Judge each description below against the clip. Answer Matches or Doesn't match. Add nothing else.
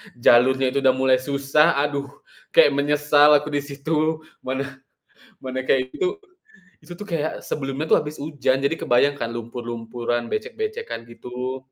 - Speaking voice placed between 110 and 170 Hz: Matches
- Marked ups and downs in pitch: Doesn't match